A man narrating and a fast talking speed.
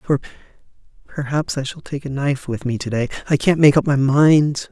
Yes: male; fast, 215 wpm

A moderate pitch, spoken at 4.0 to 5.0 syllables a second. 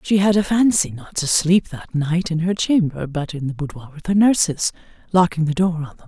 No: medium, 170 Hz; 5.4 syllables/s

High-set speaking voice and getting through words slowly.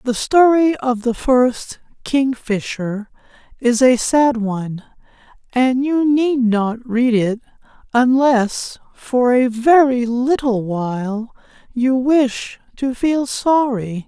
Yes: high, 245 Hz; slow, 115 wpm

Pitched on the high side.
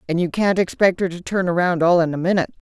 No: medium, 180 Hz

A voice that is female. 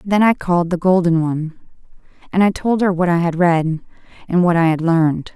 Yes: female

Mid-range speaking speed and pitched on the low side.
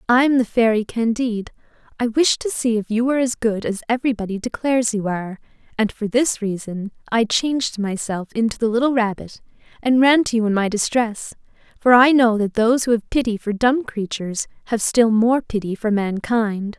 No: average, 195 wpm; high, 225 Hz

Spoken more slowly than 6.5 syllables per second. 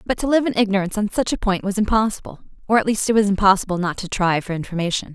No: 7.2 syllables/s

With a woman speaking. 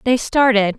Yes: female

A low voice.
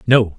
Yes: low, 110 Hz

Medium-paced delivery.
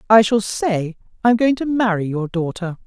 No: fast, 210 wpm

